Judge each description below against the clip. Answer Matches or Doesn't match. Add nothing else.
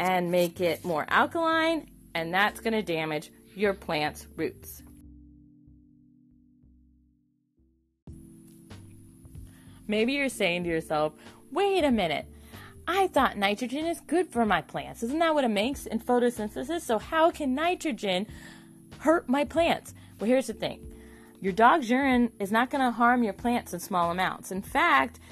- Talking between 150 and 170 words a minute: Doesn't match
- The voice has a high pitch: Matches